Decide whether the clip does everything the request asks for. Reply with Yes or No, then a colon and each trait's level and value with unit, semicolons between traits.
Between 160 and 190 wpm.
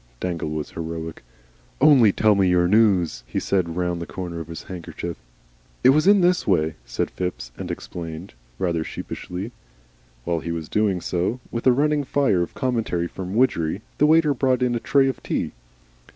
Yes: average, 180 wpm